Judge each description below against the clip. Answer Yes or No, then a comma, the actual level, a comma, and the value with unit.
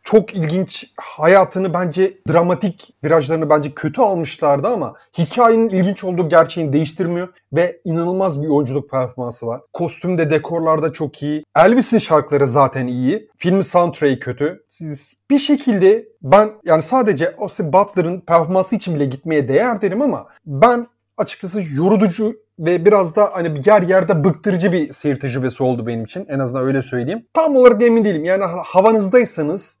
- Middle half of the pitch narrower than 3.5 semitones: No, average, 5.2 semitones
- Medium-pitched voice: Yes, medium, 175 Hz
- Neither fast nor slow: No, fast, 145 wpm